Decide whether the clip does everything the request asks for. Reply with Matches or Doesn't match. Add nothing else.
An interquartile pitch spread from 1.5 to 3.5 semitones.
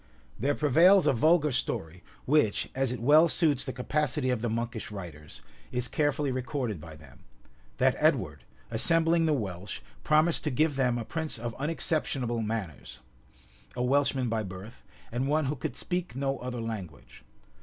Doesn't match